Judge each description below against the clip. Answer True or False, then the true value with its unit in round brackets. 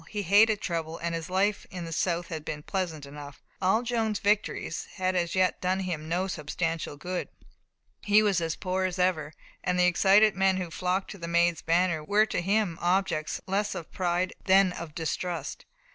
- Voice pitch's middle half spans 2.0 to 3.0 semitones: True (2.5 semitones)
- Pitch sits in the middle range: True (180 Hz)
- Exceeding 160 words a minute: True (190 wpm)